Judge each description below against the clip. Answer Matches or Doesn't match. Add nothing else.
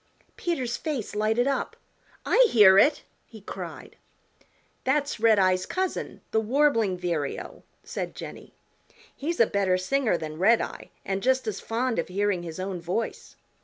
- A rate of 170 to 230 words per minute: Doesn't match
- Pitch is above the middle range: Matches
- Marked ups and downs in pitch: Matches